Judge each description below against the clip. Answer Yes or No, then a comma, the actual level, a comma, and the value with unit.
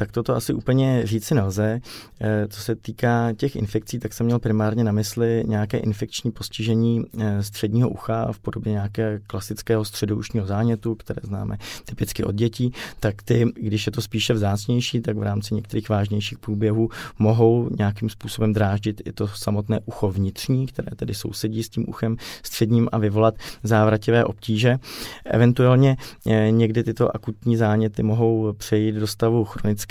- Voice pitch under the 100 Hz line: No, low, 110 Hz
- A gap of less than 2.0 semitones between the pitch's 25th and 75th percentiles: Yes, narrow, 1.6 semitones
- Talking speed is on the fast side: No, average, 155 wpm